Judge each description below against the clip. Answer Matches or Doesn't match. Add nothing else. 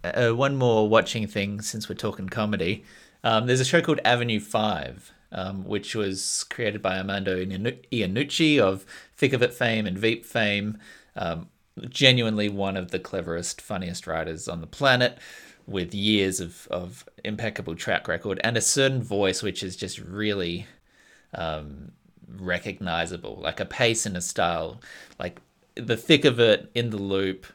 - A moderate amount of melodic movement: Matches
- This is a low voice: Matches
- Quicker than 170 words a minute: Doesn't match